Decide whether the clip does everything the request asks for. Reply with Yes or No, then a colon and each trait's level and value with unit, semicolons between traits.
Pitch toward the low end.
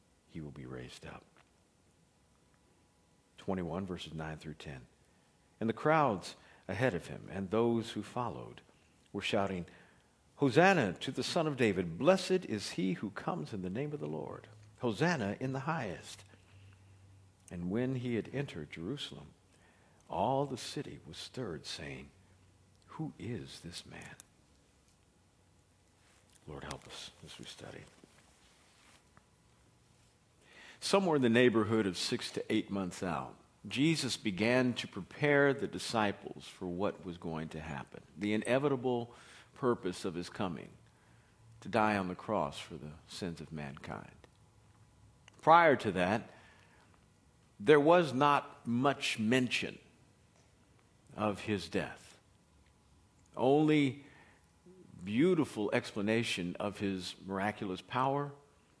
Yes: low, 105 Hz